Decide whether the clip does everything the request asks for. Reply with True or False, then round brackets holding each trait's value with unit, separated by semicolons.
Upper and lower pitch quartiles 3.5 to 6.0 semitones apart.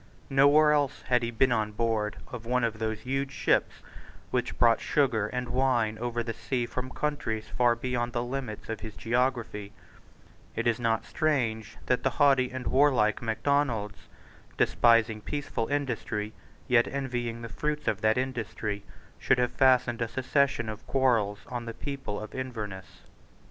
False (3.0 semitones)